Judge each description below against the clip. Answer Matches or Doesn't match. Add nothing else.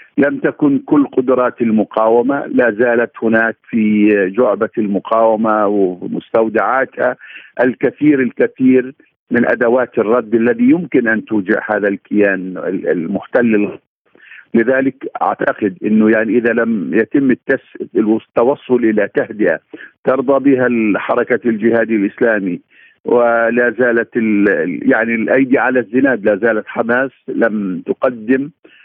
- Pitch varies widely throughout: Doesn't match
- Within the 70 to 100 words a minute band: Doesn't match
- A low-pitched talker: Matches